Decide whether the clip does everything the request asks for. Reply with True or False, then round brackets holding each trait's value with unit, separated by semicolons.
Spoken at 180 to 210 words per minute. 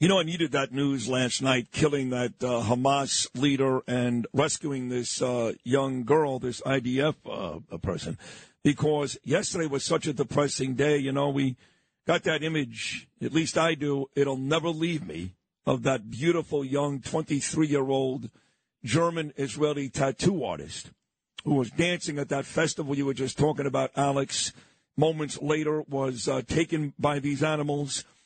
False (155 wpm)